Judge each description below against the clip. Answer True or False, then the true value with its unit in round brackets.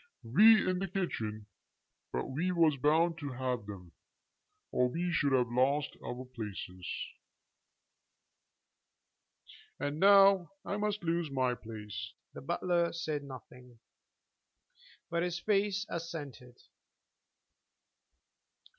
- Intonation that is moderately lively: False (5.9 semitones)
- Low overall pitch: False (145 Hz)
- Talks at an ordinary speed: False (105 wpm)